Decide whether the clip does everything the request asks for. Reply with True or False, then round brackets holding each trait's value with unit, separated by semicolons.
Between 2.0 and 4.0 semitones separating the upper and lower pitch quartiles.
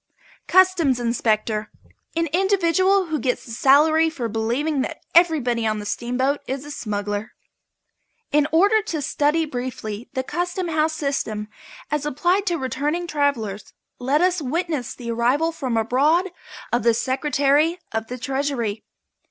False (5.5 semitones)